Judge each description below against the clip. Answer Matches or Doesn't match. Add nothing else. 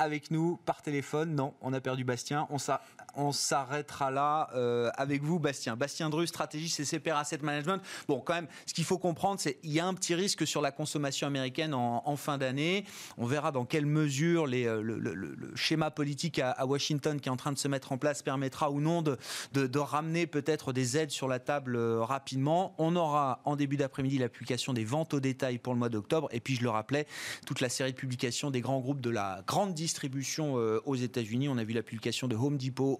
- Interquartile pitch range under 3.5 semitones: Matches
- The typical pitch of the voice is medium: Matches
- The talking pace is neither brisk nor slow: Doesn't match